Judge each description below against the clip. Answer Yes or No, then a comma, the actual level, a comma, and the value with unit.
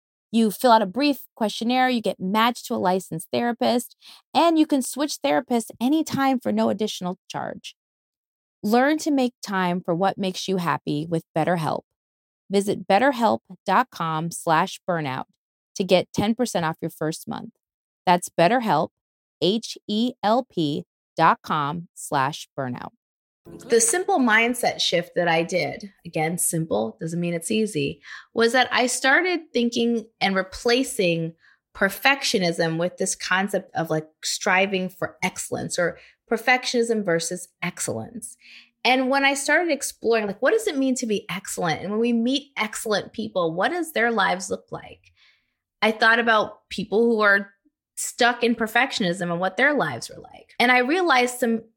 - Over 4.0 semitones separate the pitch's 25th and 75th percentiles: Yes, wide, 5.5 semitones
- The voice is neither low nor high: No, high, 215 Hz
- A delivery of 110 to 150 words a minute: Yes, average, 145 wpm